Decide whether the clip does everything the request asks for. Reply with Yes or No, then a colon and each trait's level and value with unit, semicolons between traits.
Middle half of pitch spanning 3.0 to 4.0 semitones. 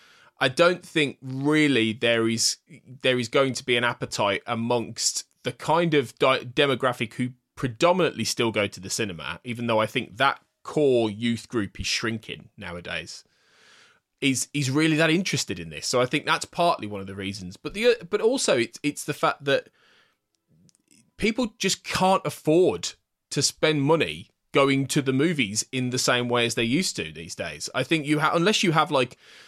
No: average, 4.9 semitones